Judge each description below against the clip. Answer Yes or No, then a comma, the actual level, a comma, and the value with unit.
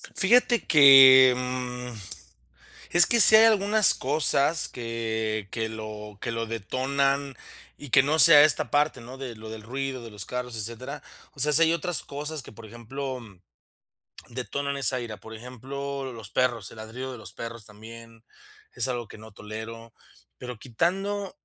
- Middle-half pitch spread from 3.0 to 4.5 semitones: Yes, average, 3.7 semitones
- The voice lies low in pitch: Yes, low, 125 Hz